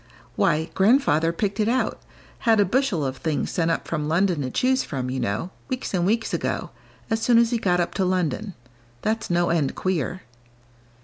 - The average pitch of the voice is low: No, medium, 180 Hz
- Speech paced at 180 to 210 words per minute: Yes, average, 190 wpm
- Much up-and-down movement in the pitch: Yes, wide, 5.7 semitones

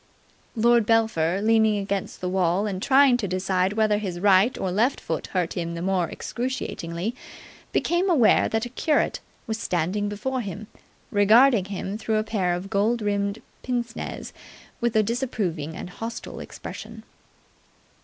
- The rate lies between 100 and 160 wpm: Yes, average, 155 wpm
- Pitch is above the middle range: Yes, high, 205 Hz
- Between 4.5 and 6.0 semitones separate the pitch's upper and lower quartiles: No, average, 3.8 semitones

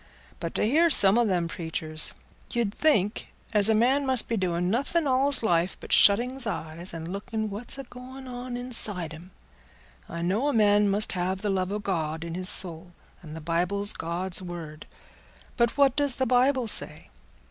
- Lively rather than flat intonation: Yes, wide, 6.0 semitones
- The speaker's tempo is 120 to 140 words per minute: No, average, 180 wpm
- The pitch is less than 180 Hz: No, high, 205 Hz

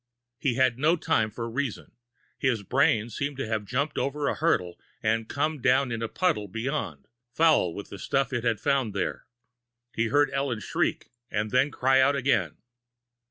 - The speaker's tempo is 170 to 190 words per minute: Yes, average, 175 wpm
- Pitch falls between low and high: No, low, 125 Hz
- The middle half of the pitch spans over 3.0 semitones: Yes, average, 4.2 semitones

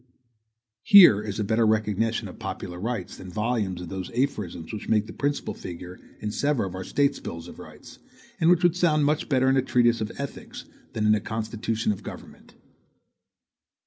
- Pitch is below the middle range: Yes, low, 110 Hz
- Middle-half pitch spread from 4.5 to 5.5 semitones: Yes, average, 5.1 semitones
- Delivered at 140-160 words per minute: No, average, 185 wpm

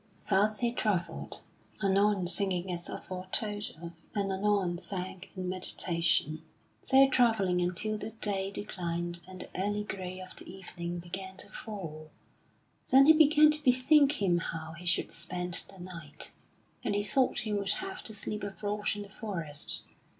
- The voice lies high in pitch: Yes, high, 195 Hz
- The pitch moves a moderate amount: Yes, average, 3.0 semitones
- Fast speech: No, average, 155 wpm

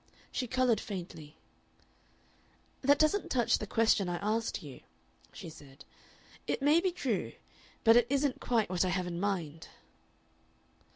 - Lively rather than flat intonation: Yes, wide, 6.5 semitones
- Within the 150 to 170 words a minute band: No, average, 140 wpm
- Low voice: No, high, 215 Hz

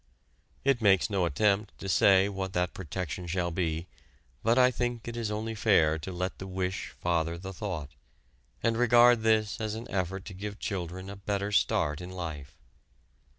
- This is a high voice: No, very low, 95 Hz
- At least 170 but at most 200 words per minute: Yes, average, 175 wpm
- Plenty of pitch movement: No, average, 3.5 semitones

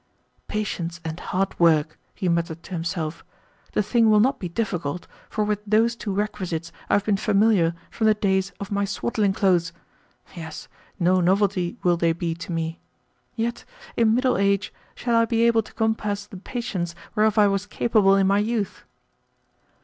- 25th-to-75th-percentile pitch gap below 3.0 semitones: No, average, 3.9 semitones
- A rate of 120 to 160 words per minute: No, average, 170 wpm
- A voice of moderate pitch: No, high, 200 Hz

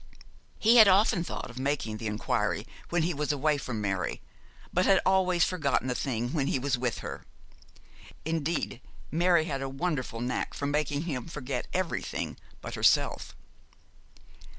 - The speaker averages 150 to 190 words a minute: Yes, average, 155 wpm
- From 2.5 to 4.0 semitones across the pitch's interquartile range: No, average, 5.2 semitones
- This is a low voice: No, medium, 145 Hz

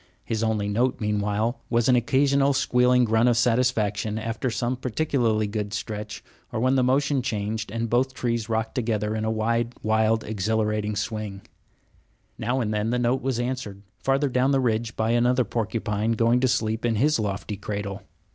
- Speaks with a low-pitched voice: Yes, low, 115 Hz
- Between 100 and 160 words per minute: No, average, 175 wpm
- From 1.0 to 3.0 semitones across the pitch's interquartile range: Yes, narrow, 2.6 semitones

